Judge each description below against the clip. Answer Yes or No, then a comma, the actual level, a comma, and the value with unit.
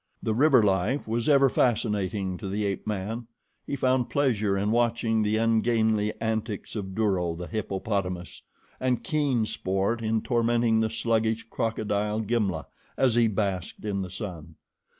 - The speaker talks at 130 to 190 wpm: Yes, average, 150 wpm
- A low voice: Yes, low, 110 Hz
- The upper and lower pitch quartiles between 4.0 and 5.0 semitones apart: No, average, 2.9 semitones